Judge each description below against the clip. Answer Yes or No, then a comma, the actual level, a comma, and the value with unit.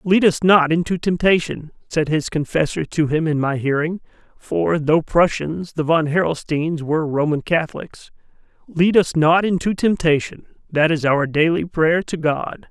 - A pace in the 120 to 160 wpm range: Yes, average, 155 wpm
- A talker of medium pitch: Yes, medium, 160 Hz